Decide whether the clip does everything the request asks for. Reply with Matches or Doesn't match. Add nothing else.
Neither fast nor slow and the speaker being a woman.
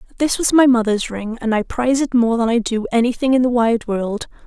Doesn't match